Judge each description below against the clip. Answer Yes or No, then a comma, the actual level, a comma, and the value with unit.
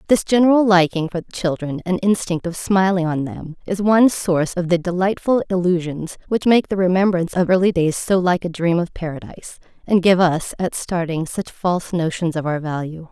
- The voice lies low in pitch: No, medium, 180 Hz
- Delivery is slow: No, average, 190 wpm